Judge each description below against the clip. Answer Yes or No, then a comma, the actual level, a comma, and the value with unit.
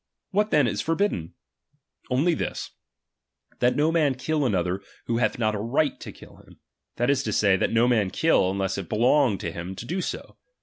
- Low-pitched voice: Yes, low, 120 Hz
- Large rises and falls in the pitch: Yes, wide, 7.1 semitones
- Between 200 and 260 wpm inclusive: Yes, fast, 205 wpm